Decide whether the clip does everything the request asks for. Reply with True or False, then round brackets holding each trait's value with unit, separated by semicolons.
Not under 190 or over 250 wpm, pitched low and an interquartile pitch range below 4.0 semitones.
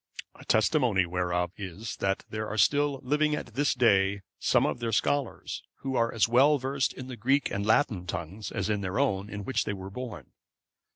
False (195 wpm; 110 Hz; 5.2 semitones)